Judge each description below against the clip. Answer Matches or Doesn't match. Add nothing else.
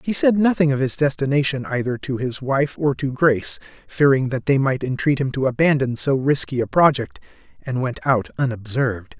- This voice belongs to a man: Matches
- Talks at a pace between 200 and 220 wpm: Doesn't match